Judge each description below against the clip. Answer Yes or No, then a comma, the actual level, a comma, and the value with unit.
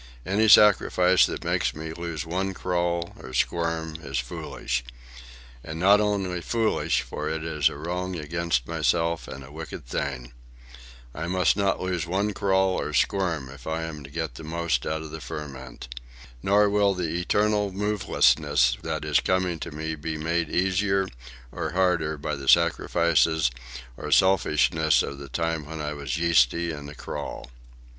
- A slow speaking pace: No, average, 160 wpm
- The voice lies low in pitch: Yes, very low, 80 Hz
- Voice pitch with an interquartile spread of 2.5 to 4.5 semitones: Yes, average, 3.8 semitones